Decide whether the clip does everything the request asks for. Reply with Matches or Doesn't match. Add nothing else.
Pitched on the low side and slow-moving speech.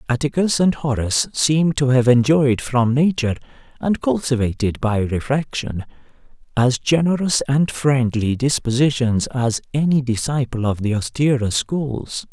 Matches